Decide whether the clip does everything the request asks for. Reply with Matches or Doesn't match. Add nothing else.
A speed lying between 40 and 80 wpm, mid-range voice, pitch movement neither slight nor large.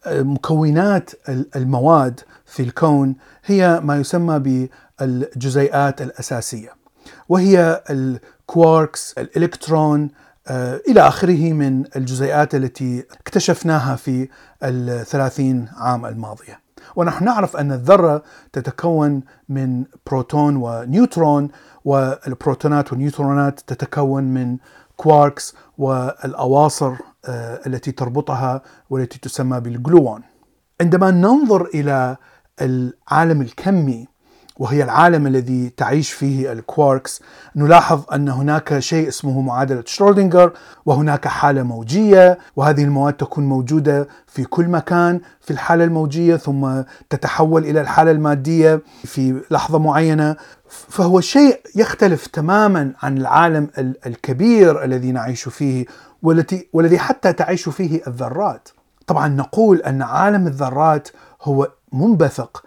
Doesn't match